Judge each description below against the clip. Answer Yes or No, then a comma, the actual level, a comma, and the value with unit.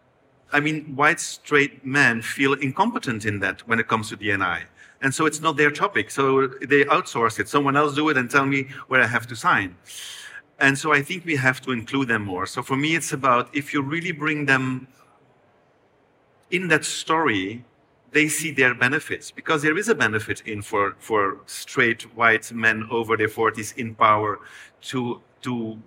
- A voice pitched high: No, low, 135 Hz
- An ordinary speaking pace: Yes, average, 190 wpm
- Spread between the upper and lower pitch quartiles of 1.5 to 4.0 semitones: No, average, 4.4 semitones